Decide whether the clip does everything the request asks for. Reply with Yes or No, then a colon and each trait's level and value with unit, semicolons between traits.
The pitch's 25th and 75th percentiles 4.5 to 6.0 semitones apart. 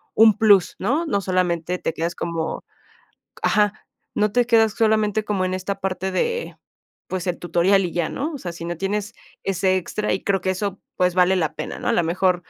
No: average, 2.9 semitones